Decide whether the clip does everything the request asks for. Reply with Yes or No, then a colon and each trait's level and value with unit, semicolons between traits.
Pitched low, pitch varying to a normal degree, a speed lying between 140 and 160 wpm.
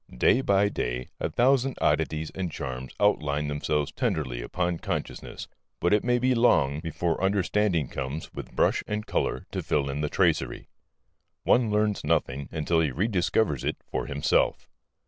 No: very low, 80 Hz; wide, 6.4 semitones; average, 155 wpm